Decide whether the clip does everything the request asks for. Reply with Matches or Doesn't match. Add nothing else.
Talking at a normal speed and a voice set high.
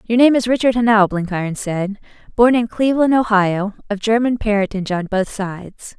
Matches